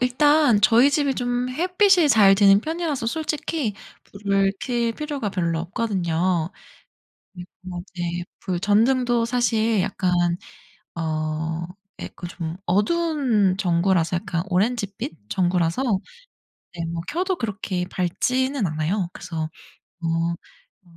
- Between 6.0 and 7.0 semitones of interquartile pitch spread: Yes, wide, 6.3 semitones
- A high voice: Yes, high, 205 Hz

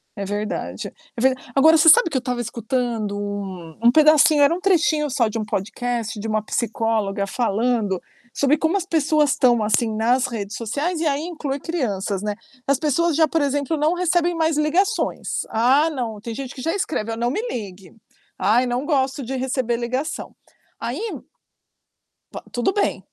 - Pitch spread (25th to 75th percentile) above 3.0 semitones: Yes, wide, 5.6 semitones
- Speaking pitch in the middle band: No, very high, 255 Hz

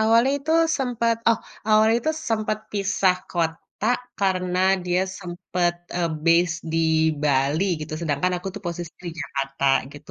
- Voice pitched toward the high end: No, medium, 180 Hz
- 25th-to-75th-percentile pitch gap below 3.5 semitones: No, average, 4.5 semitones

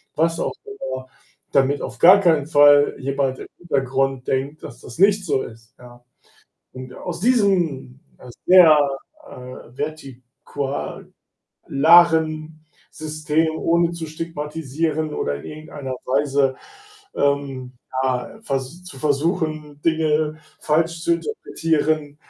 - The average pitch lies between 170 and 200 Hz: No, medium, 150 Hz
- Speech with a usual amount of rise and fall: Yes, average, 3.5 semitones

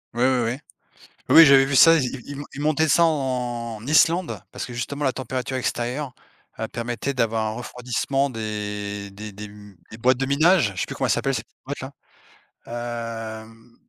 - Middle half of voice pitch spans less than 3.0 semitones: No, average, 3.6 semitones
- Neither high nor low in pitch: No, low, 120 Hz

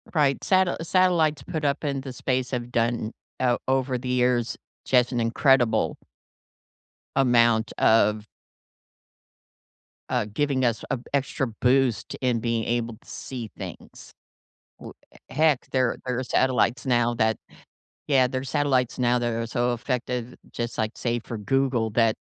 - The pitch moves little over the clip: Yes, narrow, 2.3 semitones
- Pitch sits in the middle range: No, low, 125 Hz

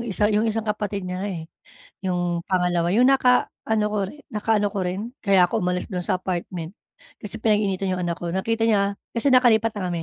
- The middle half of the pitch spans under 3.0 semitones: No, average, 3.3 semitones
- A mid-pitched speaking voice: No, high, 200 Hz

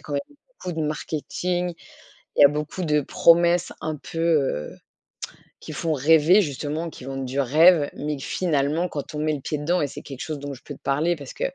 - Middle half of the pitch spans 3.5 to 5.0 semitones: No, average, 2.8 semitones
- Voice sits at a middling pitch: Yes, medium, 150 Hz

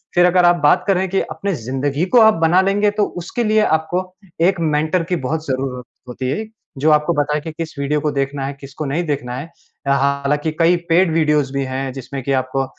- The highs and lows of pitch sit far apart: No, average, 4.3 semitones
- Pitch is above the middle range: No, medium, 150 Hz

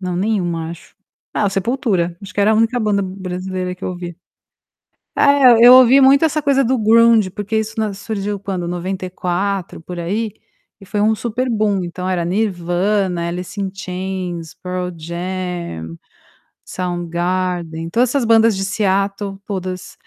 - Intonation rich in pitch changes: No, average, 3.4 semitones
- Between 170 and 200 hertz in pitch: Yes, high, 190 Hz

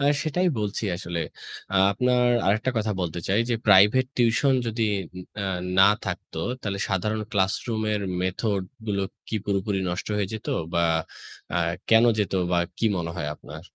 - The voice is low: Yes, low, 105 Hz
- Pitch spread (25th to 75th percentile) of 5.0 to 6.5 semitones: No, average, 3.2 semitones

